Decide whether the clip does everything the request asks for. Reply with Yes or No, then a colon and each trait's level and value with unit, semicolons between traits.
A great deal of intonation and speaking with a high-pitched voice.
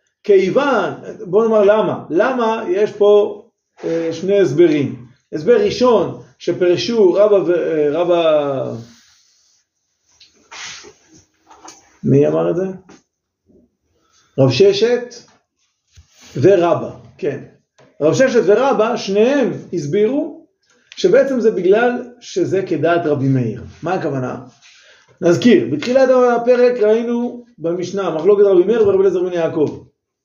Yes: wide, 6.7 semitones; high, 205 Hz